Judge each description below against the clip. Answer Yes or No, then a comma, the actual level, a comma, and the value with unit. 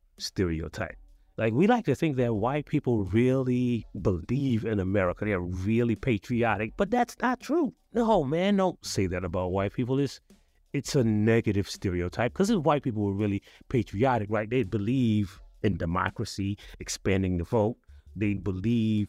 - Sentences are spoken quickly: No, average, 155 wpm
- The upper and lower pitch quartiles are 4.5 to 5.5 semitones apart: Yes, average, 5.1 semitones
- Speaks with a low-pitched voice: Yes, low, 110 Hz